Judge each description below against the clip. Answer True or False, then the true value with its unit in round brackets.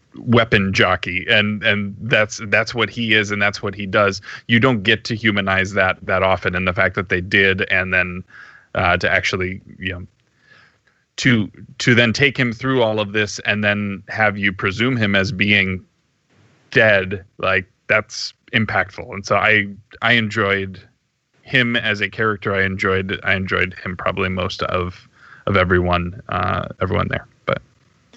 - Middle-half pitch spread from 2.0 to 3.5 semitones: True (2.8 semitones)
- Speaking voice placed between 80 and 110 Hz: True (100 Hz)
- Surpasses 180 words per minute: False (165 wpm)